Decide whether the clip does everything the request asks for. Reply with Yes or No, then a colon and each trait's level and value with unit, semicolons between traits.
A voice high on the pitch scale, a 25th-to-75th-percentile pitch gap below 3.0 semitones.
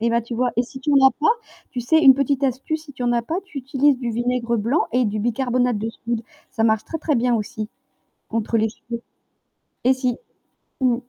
Yes: high, 245 Hz; narrow, 2.5 semitones